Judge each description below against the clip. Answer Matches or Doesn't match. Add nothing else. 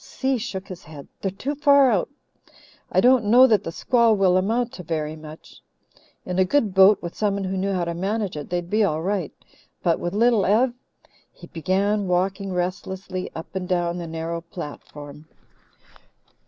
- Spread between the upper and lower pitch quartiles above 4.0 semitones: Doesn't match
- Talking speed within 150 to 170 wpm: Doesn't match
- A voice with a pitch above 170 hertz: Matches